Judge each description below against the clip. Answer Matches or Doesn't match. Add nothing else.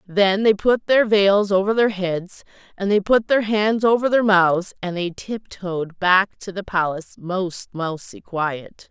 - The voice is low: Doesn't match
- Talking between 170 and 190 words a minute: Matches